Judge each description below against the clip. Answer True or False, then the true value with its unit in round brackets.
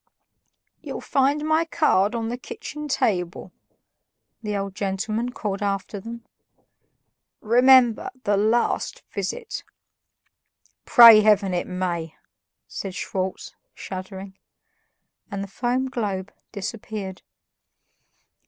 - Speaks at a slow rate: True (95 wpm)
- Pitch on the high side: True (210 Hz)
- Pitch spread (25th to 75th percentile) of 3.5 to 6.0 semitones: True (3.9 semitones)